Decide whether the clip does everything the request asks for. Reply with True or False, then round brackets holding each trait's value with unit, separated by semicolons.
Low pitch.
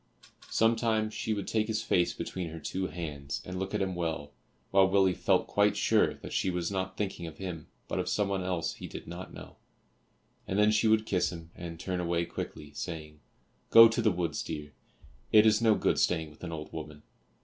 True (90 Hz)